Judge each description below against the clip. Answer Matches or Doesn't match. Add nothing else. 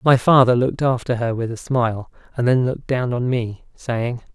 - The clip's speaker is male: Matches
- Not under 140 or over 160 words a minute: Doesn't match